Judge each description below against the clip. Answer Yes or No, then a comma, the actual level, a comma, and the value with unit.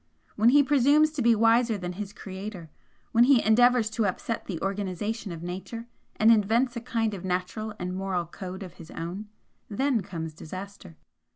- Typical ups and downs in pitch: Yes, average, 4.0 semitones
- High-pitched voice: Yes, high, 210 Hz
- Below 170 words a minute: No, average, 175 wpm